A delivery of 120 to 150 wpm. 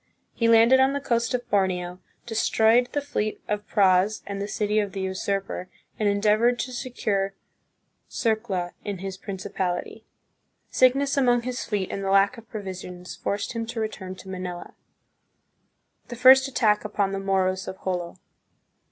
No: average, 160 wpm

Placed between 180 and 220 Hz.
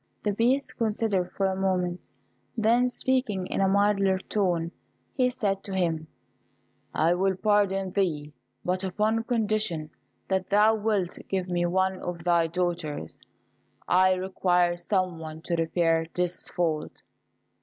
Yes: medium, 185 Hz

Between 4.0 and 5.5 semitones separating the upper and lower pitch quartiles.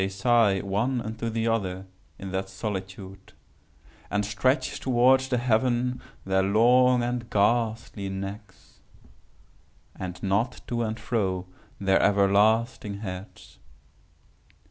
No: average, 3.6 semitones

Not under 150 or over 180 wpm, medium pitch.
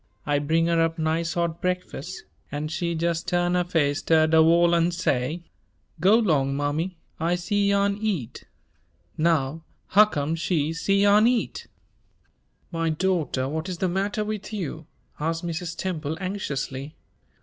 No: average, 140 wpm; medium, 170 Hz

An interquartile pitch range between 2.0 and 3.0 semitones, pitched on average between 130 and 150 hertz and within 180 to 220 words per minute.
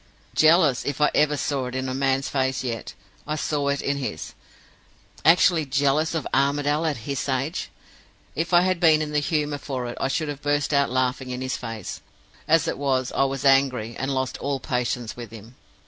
Yes: narrow, 2.4 semitones; medium, 140 Hz; average, 200 wpm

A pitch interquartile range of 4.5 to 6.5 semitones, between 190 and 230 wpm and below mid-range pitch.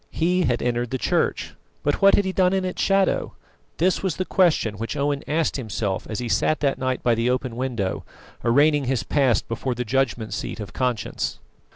Yes: average, 5.1 semitones; average, 200 wpm; low, 130 Hz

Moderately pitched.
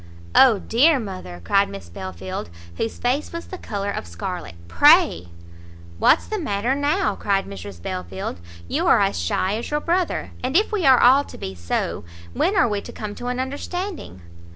No: high, 210 Hz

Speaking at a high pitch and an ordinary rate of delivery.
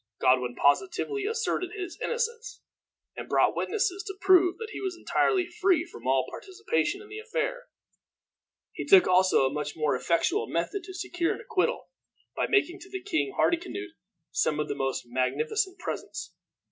Yes: very high, 370 Hz; average, 150 wpm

